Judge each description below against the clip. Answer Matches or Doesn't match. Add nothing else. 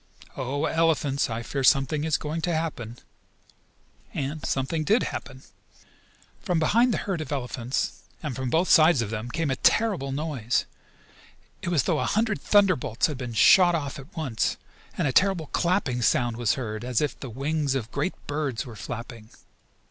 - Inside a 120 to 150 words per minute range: Doesn't match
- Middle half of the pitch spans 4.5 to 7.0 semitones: Matches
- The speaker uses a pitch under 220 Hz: Matches